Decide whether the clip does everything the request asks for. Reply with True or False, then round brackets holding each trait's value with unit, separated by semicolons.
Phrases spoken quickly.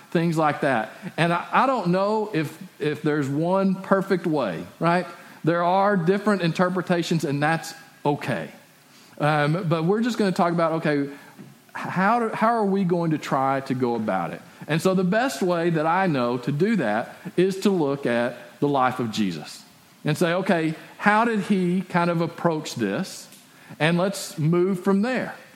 False (180 wpm)